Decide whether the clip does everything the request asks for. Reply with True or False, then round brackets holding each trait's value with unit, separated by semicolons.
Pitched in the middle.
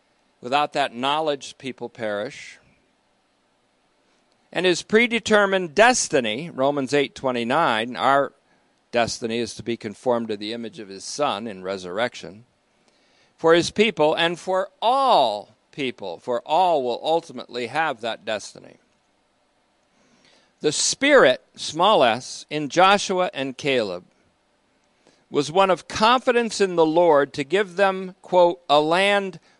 True (150 Hz)